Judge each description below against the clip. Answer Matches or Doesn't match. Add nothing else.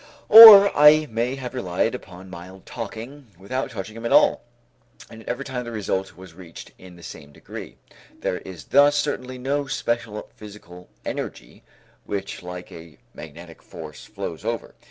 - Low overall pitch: Matches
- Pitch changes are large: Matches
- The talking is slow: Doesn't match